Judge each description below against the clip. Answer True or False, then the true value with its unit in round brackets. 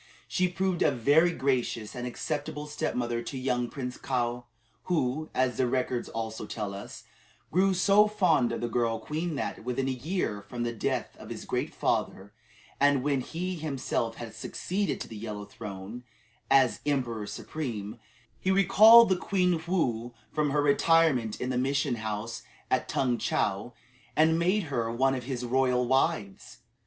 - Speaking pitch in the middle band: False (130 Hz)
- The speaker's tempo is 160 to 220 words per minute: True (165 wpm)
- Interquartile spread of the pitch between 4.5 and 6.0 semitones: True (5.1 semitones)